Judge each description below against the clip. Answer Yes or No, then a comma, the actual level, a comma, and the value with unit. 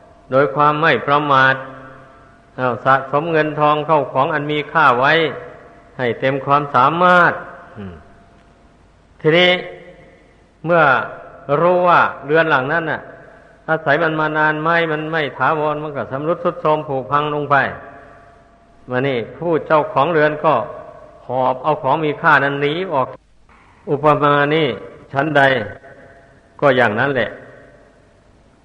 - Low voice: No, medium, 145 Hz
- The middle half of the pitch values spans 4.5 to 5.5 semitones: No, average, 2.8 semitones